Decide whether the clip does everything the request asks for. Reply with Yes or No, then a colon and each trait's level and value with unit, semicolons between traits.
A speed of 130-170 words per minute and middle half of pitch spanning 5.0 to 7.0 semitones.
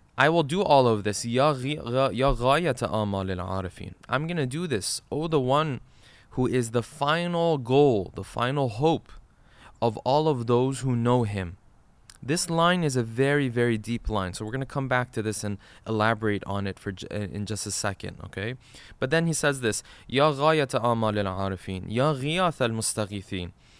Yes: average, 145 wpm; wide, 5.4 semitones